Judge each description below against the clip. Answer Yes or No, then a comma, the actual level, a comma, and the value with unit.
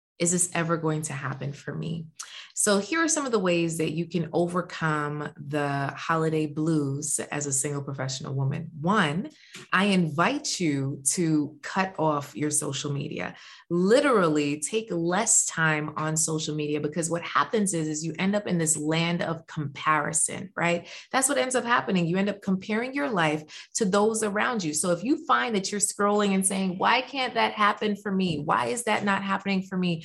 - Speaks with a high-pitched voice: No, medium, 170 Hz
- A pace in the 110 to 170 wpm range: No, average, 190 wpm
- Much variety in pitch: No, average, 4.9 semitones